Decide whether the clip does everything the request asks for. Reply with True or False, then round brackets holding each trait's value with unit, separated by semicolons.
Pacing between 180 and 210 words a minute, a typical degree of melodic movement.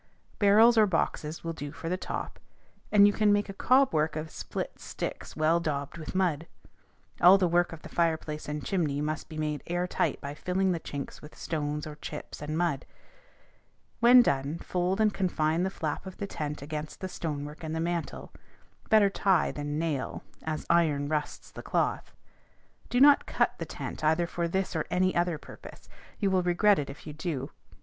True (190 wpm; 3.7 semitones)